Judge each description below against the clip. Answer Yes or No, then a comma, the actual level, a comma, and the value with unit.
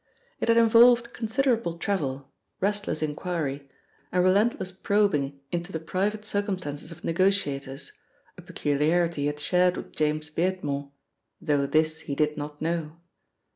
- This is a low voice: No, medium, 170 Hz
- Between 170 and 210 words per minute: No, slow, 135 wpm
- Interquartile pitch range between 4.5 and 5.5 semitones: Yes, average, 5.2 semitones